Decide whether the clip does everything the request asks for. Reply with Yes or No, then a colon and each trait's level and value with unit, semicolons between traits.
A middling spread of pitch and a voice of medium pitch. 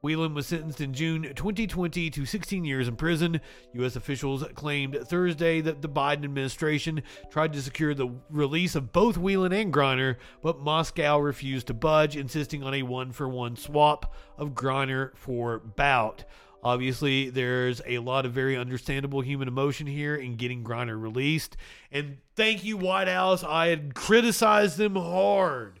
Yes: average, 3.7 semitones; medium, 145 Hz